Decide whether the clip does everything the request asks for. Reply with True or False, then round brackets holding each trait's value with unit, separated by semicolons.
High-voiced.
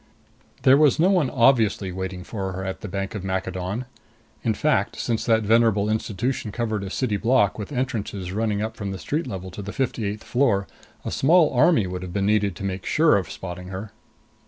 False (105 Hz)